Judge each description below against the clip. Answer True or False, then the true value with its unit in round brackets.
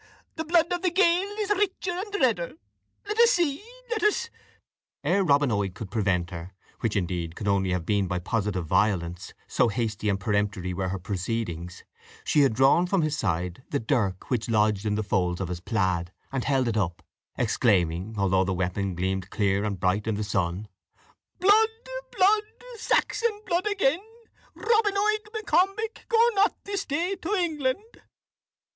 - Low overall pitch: True (110 Hz)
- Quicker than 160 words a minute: True (170 wpm)